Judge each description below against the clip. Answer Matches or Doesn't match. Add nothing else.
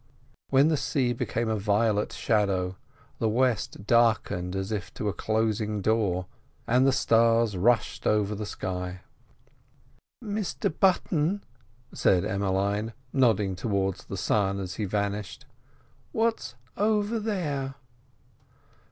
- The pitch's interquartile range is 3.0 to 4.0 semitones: Doesn't match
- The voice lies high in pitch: Doesn't match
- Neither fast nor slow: Doesn't match